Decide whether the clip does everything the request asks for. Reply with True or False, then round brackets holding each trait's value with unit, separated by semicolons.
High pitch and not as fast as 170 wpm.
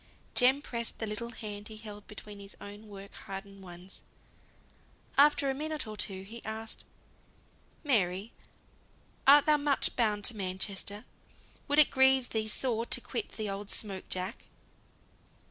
True (215 Hz; 145 wpm)